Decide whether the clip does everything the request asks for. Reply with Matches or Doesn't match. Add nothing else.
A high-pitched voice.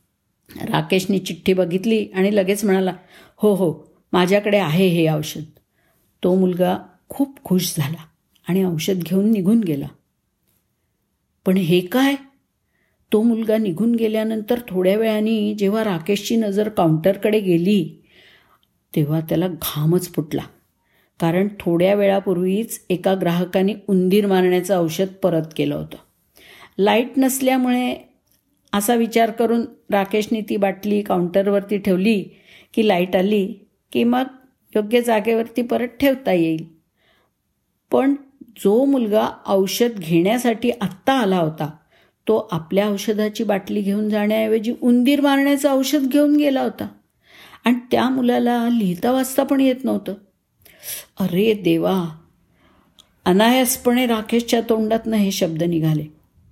Matches